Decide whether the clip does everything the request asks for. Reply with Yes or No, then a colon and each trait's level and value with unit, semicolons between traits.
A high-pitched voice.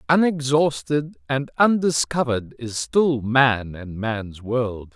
No: low, 130 Hz